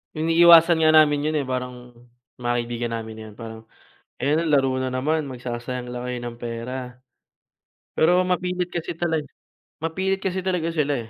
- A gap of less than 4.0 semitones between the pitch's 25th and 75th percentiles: No, average, 5.2 semitones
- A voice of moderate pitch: Yes, medium, 145 Hz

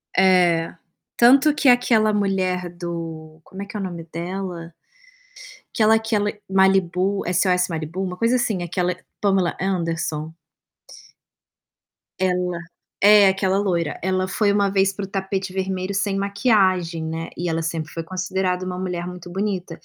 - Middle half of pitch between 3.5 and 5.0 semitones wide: No, narrow, 2.4 semitones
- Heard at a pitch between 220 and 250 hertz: No, medium, 185 Hz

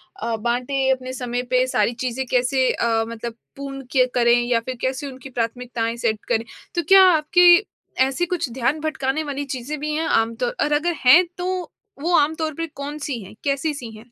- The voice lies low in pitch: No, very high, 265 Hz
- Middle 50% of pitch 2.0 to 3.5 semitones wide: No, average, 3.9 semitones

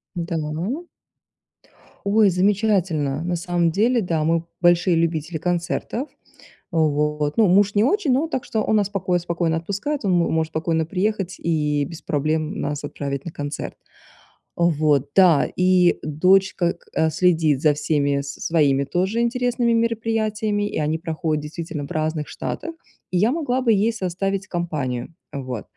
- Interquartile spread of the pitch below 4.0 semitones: No, average, 4.8 semitones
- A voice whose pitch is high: No, medium, 170 Hz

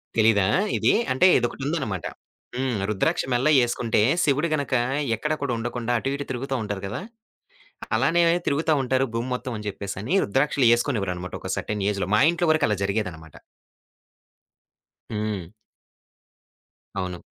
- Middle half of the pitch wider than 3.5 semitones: Yes, average, 4.9 semitones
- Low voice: Yes, low, 120 Hz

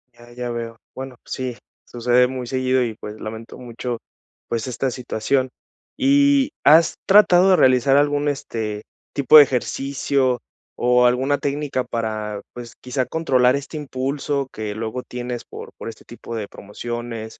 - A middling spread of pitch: Yes, average, 3.0 semitones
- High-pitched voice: No, low, 125 Hz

